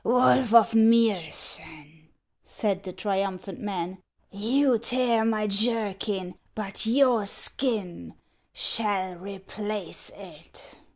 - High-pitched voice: Yes, high, 210 Hz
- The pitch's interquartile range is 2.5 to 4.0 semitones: Yes, average, 3.3 semitones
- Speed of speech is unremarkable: No, slow, 100 wpm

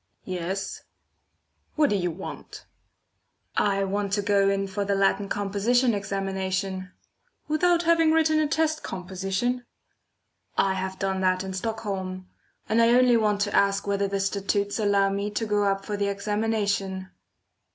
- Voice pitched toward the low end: No, high, 200 Hz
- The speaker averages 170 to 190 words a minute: No, average, 150 wpm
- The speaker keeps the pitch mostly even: Yes, narrow, 2.2 semitones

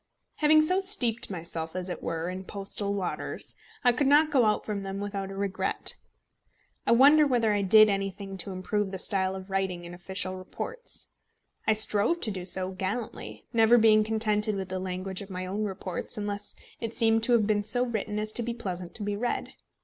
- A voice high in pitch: Yes, high, 205 Hz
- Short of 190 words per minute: No, average, 200 wpm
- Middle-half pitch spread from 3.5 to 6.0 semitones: No, average, 3.1 semitones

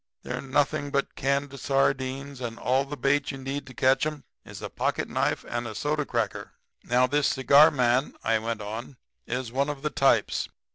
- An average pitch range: No, narrow, 2.0 semitones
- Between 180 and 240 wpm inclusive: Yes, average, 185 wpm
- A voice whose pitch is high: No, low, 135 Hz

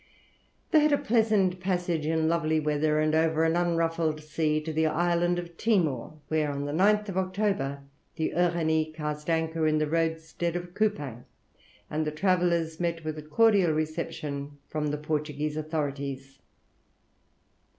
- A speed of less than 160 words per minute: Yes, average, 150 wpm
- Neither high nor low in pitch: Yes, medium, 160 Hz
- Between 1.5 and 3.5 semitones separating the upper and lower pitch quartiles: Yes, narrow, 2.4 semitones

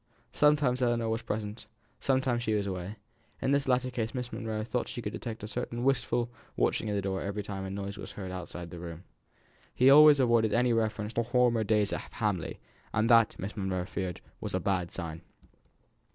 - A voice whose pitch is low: Yes, low, 110 Hz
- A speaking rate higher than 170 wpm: Yes, average, 195 wpm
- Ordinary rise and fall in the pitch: Yes, average, 3.8 semitones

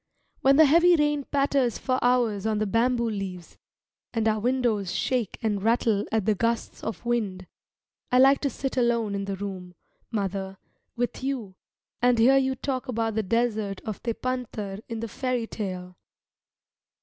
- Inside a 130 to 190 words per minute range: Yes, average, 160 wpm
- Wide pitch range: No, average, 3.9 semitones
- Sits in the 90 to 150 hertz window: No, high, 230 Hz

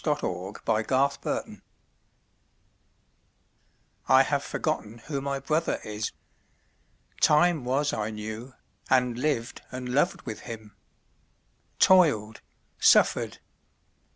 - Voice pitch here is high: No, low, 125 Hz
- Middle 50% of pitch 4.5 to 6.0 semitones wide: Yes, average, 4.8 semitones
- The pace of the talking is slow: Yes, slow, 100 wpm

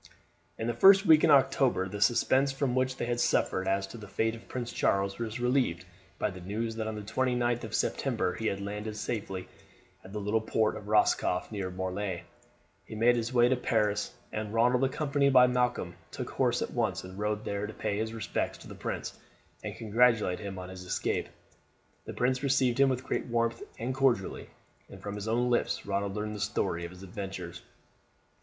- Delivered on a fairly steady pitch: No, average, 3.8 semitones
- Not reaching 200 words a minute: No, fast, 205 wpm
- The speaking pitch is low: Yes, low, 110 Hz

